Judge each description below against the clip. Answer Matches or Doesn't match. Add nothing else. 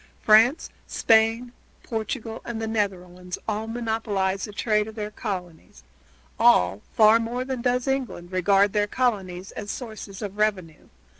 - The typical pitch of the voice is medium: Doesn't match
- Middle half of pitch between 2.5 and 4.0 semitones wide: Matches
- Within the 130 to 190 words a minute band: Matches